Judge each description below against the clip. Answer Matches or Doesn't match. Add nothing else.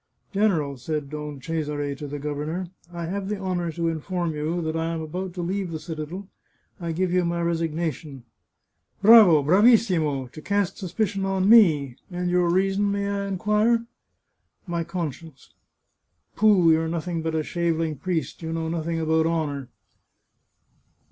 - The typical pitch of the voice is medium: Matches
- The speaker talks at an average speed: Matches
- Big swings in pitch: Doesn't match